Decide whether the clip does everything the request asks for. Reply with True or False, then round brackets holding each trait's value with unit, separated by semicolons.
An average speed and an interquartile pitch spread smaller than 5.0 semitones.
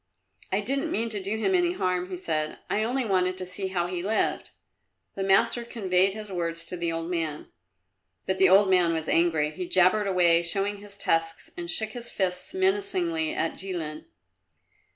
True (185 wpm; 3.9 semitones)